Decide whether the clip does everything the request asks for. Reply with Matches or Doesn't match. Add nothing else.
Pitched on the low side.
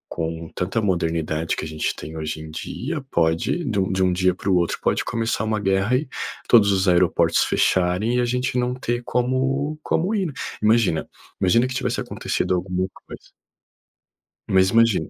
Matches